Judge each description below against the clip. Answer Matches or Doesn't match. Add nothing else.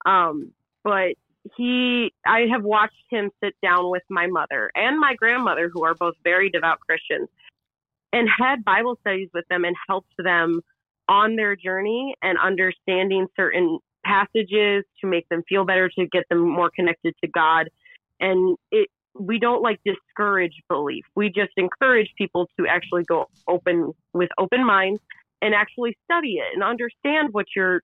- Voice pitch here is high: Matches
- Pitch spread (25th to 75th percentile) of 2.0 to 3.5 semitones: Doesn't match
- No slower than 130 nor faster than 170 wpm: Matches